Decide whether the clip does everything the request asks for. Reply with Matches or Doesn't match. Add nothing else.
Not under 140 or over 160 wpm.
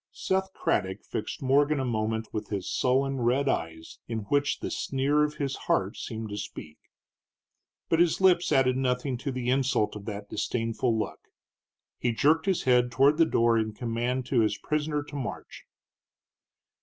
Doesn't match